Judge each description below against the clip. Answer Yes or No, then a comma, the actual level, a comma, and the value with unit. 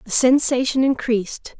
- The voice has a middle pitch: No, high, 245 Hz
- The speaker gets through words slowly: Yes, slow, 115 wpm